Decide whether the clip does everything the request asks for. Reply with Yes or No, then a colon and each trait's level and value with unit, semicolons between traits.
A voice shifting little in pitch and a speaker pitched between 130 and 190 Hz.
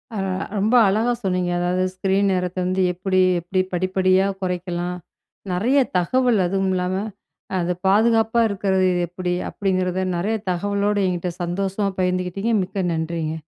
Yes: narrow, 1.9 semitones; medium, 185 Hz